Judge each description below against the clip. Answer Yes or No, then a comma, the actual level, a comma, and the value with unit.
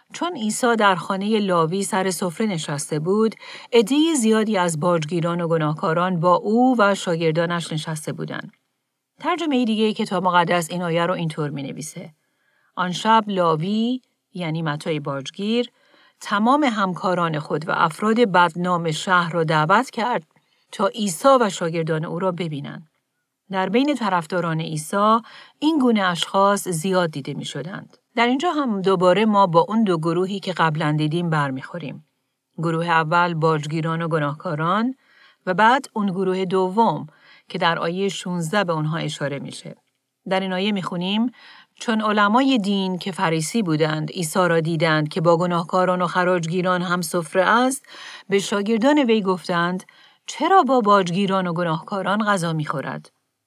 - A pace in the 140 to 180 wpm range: Yes, average, 145 wpm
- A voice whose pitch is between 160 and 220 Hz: Yes, medium, 185 Hz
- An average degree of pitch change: Yes, average, 4.3 semitones